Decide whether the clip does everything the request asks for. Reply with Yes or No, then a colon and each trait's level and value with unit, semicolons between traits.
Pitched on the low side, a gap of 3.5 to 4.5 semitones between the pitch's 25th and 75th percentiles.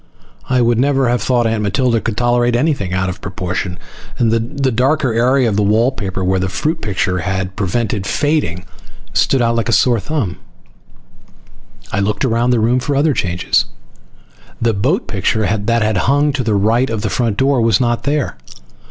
Yes: low, 115 Hz; average, 4.2 semitones